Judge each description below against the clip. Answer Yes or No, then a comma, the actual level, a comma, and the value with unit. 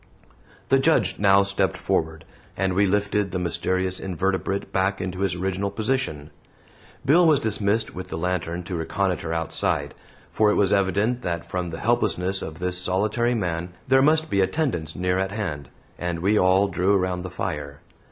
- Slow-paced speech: No, average, 170 wpm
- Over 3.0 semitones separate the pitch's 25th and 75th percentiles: No, narrow, 2.5 semitones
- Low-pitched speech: Yes, very low, 95 Hz